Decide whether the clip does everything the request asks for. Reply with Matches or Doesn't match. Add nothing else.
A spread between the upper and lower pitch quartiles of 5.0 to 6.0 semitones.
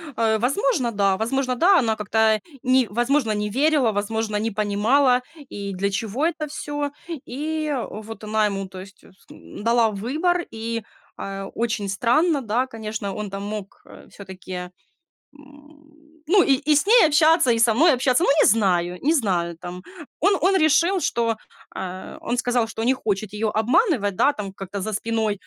Matches